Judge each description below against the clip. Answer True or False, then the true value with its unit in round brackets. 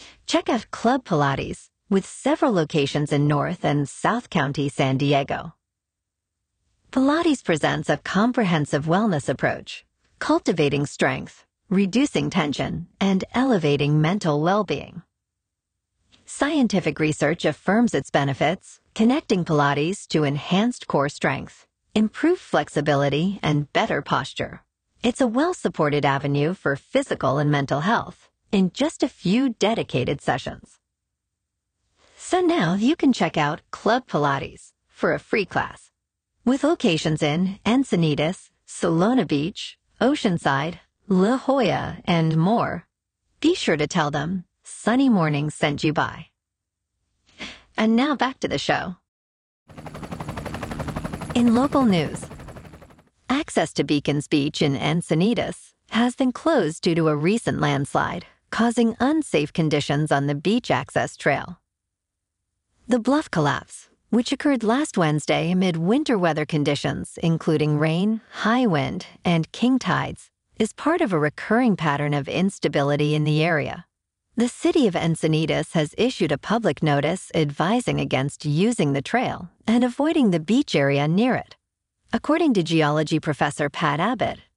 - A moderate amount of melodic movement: False (8.1 semitones)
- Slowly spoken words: True (130 wpm)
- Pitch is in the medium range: True (170 Hz)